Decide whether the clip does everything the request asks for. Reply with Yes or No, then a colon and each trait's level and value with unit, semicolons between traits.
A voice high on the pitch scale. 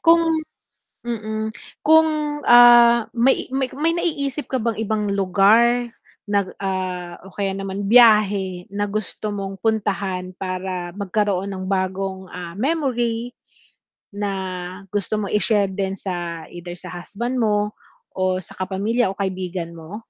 Yes: high, 205 Hz